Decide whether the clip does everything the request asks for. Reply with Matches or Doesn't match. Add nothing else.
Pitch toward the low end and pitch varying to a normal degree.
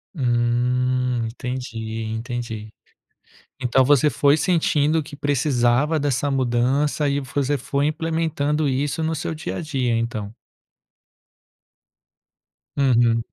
Matches